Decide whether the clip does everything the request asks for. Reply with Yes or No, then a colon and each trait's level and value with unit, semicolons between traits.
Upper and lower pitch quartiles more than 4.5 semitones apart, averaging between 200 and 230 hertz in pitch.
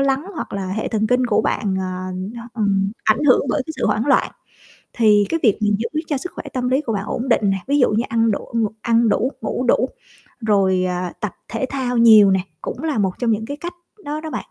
No: average, 4.2 semitones; high, 225 Hz